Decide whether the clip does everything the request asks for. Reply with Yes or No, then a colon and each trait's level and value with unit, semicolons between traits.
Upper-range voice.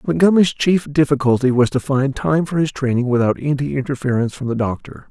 No: low, 135 Hz